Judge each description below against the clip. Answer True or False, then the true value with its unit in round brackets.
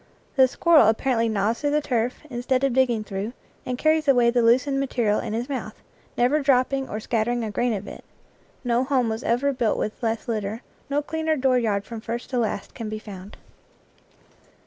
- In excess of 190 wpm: True (205 wpm)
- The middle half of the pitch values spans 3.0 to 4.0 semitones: True (3.3 semitones)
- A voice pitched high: True (240 Hz)